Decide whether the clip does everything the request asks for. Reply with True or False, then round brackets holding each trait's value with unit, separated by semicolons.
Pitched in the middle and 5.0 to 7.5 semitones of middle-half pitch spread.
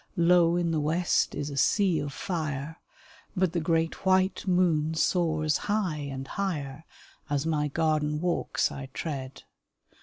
False (160 Hz; 3.0 semitones)